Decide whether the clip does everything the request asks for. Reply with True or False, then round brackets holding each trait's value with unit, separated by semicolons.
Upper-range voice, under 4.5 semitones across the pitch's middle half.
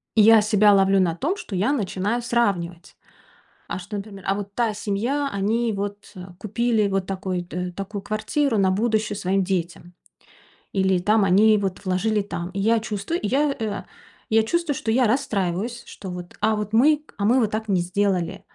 True (205 Hz; 2.8 semitones)